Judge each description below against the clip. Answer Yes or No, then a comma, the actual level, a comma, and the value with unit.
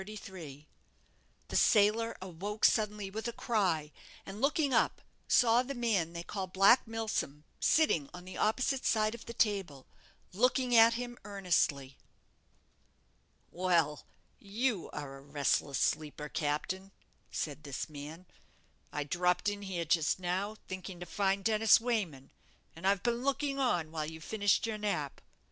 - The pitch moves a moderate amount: No, wide, 5.8 semitones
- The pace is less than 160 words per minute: Yes, average, 140 wpm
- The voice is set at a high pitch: Yes, high, 195 Hz